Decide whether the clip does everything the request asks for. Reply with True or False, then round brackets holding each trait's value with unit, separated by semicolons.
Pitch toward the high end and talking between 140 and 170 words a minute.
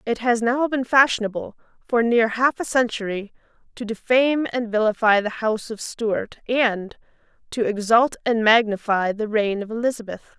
True (230 Hz; 155 wpm)